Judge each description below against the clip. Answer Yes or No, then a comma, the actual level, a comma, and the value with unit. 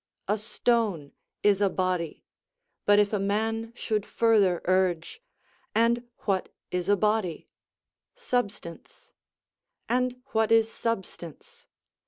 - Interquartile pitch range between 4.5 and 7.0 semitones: No, average, 3.4 semitones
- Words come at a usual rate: No, slow, 110 wpm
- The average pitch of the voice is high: Yes, high, 210 Hz